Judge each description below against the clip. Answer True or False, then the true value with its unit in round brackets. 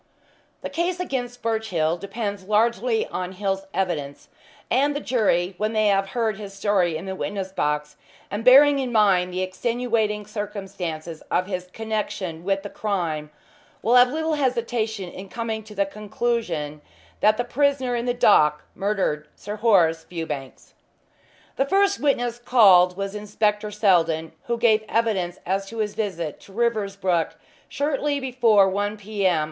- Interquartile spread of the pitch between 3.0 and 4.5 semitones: True (4.2 semitones)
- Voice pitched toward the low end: False (205 Hz)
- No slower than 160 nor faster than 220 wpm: False (150 wpm)